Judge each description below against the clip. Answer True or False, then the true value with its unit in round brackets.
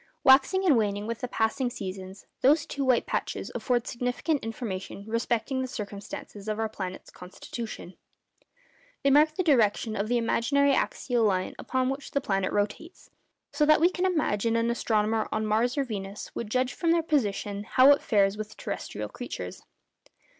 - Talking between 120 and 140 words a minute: False (170 wpm)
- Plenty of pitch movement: False (4.9 semitones)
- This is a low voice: False (230 Hz)